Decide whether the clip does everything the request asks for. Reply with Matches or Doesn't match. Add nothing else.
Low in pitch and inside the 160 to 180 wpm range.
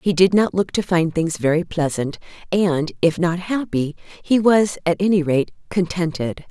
Doesn't match